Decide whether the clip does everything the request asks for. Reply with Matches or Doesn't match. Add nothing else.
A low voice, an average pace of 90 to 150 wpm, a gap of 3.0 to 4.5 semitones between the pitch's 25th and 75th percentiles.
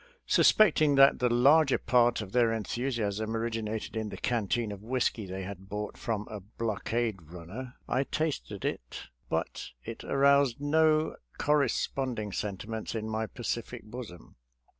Matches